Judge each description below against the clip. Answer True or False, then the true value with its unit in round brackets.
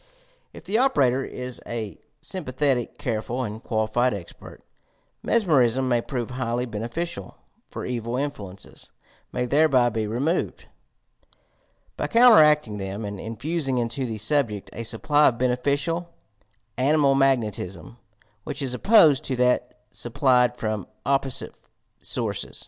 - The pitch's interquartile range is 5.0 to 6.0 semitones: False (3.8 semitones)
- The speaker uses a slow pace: True (125 wpm)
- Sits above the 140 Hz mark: False (125 Hz)